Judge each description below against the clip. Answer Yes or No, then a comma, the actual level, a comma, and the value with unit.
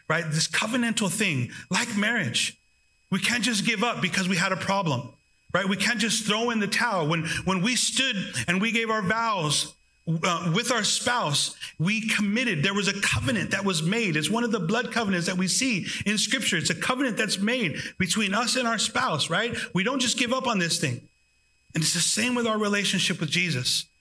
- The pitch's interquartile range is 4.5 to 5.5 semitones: Yes, average, 4.8 semitones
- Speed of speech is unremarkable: No, fast, 210 wpm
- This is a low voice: No, high, 200 Hz